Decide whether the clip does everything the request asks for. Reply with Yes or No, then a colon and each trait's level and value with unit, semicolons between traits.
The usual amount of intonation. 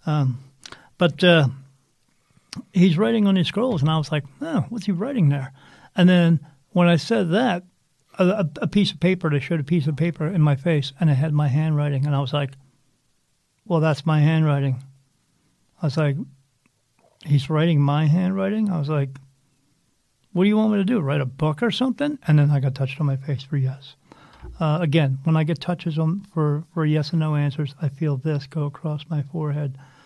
Yes: average, 3.7 semitones